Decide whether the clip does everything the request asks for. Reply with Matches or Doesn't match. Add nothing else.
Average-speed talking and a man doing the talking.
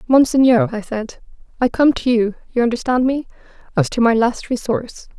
Doesn't match